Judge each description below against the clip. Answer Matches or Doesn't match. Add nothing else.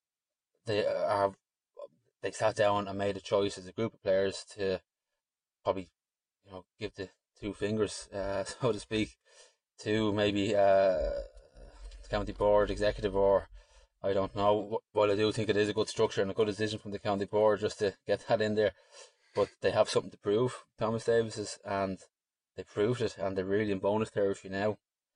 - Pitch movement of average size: Doesn't match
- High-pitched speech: Doesn't match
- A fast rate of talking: Doesn't match